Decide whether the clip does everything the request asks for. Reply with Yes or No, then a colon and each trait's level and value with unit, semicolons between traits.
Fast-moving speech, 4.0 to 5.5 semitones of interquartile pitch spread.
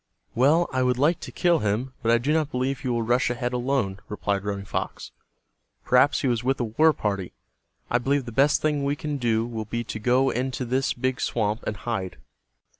No: fast, 210 wpm; average, 3.3 semitones